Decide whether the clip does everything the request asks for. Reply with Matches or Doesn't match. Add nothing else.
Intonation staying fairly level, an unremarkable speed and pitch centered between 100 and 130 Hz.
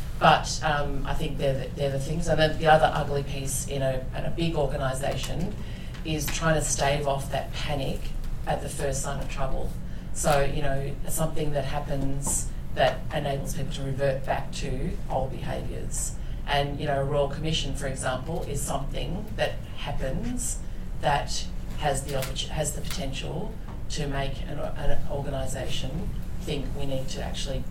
Doesn't match